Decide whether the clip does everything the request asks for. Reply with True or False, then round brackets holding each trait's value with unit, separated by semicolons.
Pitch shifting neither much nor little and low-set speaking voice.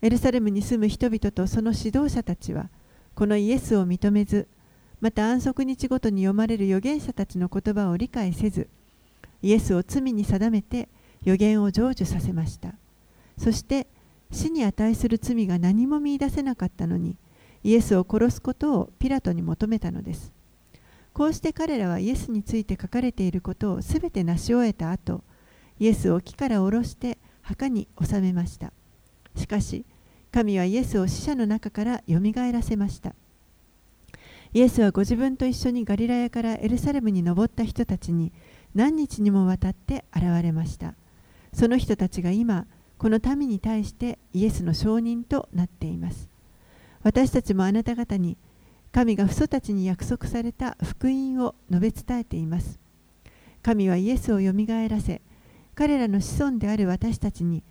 False (4.8 semitones; 215 Hz)